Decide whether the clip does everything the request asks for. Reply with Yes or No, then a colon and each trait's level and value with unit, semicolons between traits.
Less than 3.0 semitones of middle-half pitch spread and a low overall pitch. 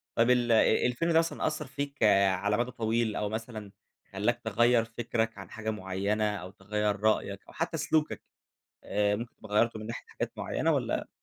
Yes: narrow, 2.6 semitones; low, 110 Hz